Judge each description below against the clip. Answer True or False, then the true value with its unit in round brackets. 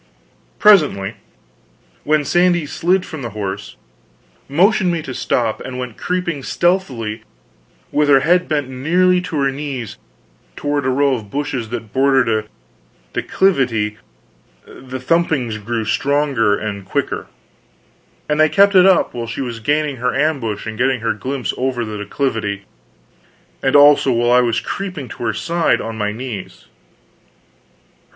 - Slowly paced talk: False (145 wpm)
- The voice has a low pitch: True (130 Hz)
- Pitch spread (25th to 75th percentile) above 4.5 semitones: True (5.2 semitones)